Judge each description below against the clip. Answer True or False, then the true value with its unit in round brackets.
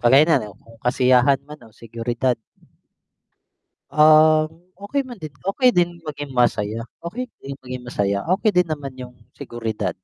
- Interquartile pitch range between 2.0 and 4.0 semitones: False (5.0 semitones)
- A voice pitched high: False (140 Hz)